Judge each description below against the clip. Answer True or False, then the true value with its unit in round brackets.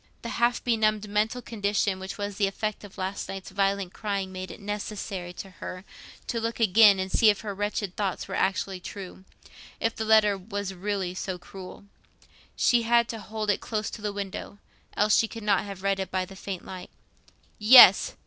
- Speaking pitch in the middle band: False (200 Hz)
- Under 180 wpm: False (195 wpm)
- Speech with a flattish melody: True (2.1 semitones)